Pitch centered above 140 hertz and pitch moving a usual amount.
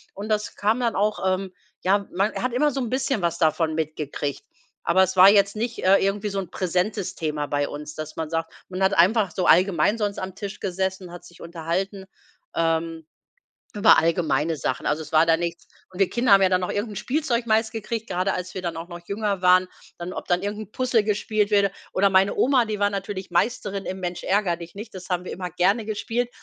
Yes: high, 190 Hz; average, 3.3 semitones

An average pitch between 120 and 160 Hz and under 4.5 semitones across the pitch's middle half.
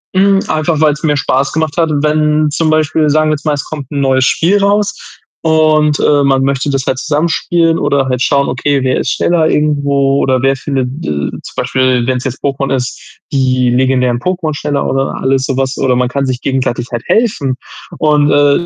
Yes: medium, 140 Hz; average, 2.8 semitones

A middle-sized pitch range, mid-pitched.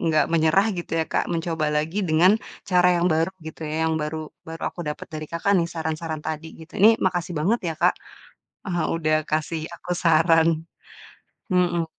No: narrow, 1.8 semitones; medium, 165 Hz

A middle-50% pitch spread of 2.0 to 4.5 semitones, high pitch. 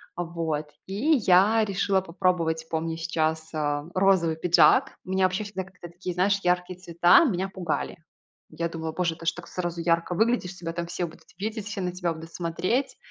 No: narrow, 2.4 semitones; medium, 175 Hz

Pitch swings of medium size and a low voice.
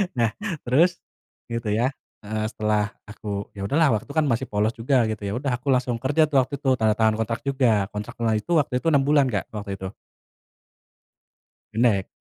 Yes: average, 4.2 semitones; low, 115 Hz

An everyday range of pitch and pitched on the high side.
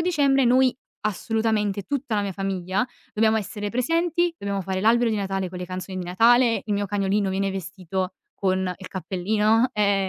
Yes: average, 3.4 semitones; high, 205 Hz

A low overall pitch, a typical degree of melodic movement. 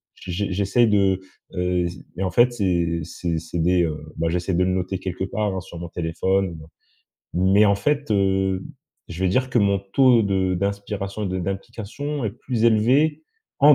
Yes: very low, 95 Hz; average, 3.2 semitones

